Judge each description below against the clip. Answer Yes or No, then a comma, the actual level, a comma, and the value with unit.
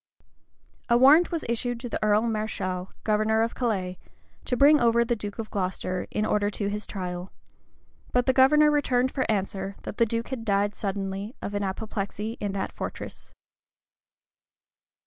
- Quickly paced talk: No, average, 165 wpm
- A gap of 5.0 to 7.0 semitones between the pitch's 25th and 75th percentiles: No, average, 3.4 semitones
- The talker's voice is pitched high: Yes, high, 215 Hz